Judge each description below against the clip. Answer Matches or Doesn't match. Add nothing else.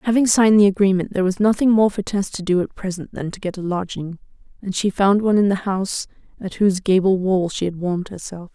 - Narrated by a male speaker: Doesn't match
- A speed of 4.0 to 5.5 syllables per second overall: Doesn't match